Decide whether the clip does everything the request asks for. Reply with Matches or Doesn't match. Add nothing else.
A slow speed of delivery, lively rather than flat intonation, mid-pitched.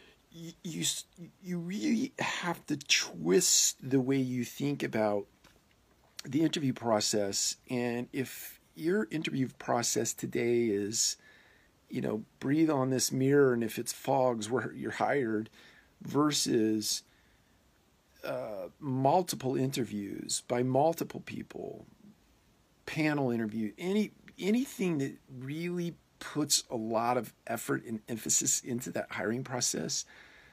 Doesn't match